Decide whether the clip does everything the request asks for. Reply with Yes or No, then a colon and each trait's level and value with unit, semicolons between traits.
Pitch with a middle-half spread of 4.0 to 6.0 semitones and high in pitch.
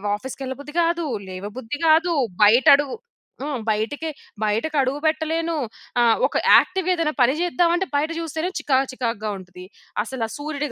Yes: wide, 5.6 semitones; very high, 285 Hz